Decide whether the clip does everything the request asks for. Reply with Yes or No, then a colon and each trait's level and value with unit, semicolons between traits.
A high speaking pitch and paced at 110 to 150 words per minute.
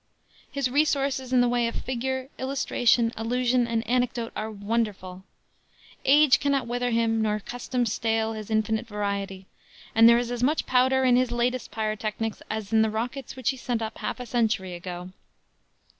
No: high, 235 Hz; average, 170 wpm